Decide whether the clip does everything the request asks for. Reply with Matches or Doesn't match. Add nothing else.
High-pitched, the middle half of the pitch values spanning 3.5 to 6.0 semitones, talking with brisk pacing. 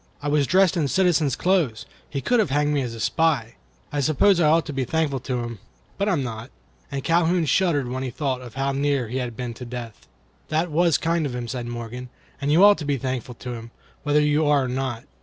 Doesn't match